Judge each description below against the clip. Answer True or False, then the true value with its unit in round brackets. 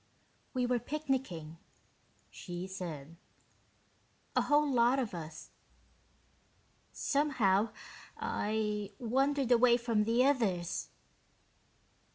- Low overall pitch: False (230 Hz)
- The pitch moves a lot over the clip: True (5.8 semitones)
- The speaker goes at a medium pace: False (85 wpm)